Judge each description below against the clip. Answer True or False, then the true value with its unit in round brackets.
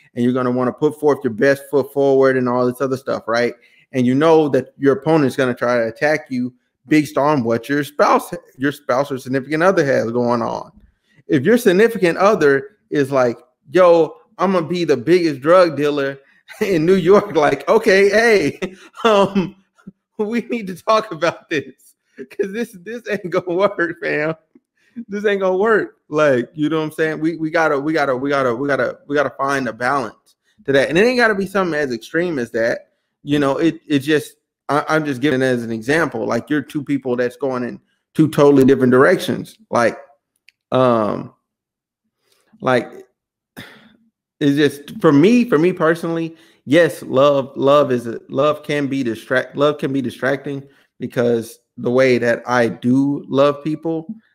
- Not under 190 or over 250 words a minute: False (180 wpm)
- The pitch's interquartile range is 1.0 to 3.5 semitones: False (5.3 semitones)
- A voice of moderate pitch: True (150 Hz)